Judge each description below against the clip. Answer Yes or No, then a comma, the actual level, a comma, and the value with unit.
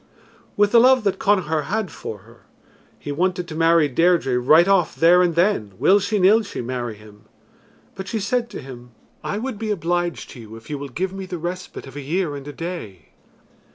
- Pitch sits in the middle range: Yes, medium, 170 Hz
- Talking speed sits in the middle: No, fast, 210 wpm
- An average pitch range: No, wide, 6.1 semitones